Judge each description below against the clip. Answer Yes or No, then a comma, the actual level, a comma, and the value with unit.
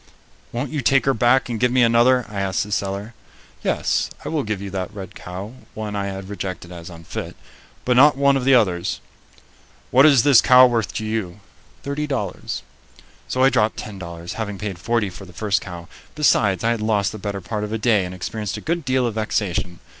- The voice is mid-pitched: No, low, 105 Hz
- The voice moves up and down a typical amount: Yes, average, 4.4 semitones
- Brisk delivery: Yes, fast, 215 wpm